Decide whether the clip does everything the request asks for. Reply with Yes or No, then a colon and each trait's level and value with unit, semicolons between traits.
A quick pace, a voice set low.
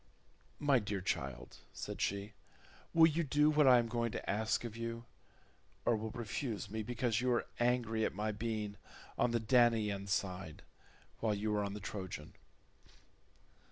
No: average, 165 wpm; low, 110 Hz